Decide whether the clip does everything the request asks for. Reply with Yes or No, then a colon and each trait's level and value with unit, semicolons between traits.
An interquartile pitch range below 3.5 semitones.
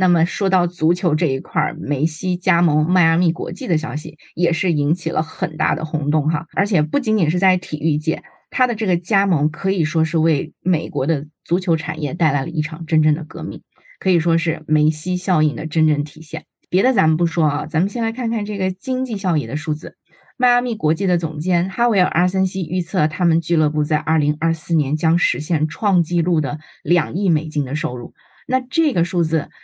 Yes: average, 2.9 semitones